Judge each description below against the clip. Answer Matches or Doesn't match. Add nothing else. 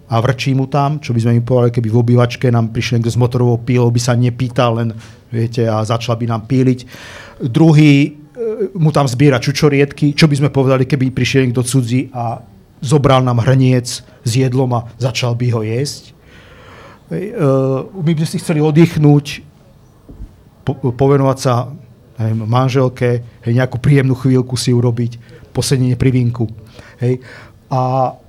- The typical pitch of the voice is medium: Doesn't match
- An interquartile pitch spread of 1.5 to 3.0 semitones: Matches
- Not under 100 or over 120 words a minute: Doesn't match